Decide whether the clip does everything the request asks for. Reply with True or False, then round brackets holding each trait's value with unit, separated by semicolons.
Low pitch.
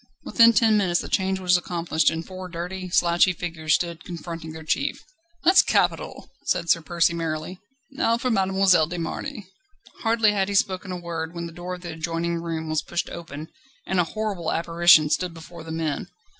False (175 Hz)